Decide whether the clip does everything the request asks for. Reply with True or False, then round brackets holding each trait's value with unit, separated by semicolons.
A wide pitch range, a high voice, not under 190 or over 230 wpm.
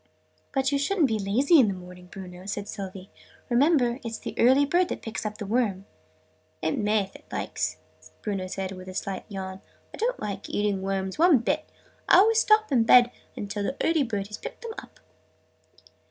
True (6.1 semitones; 210 Hz; 195 wpm)